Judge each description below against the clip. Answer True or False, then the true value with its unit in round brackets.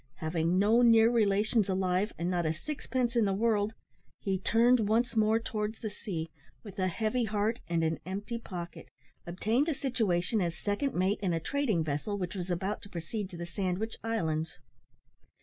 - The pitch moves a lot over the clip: False (4.2 semitones)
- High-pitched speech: True (205 Hz)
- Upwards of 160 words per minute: True (180 wpm)